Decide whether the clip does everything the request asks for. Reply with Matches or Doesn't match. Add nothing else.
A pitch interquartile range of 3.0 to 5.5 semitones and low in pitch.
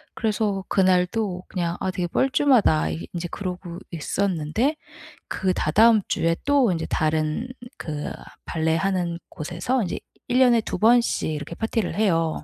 Doesn't match